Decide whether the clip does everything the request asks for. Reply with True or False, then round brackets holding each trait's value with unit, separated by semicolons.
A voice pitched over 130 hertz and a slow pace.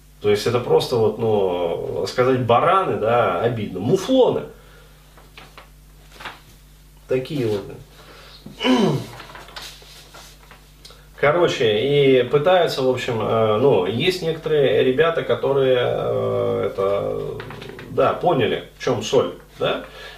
True (140 Hz; 90 wpm)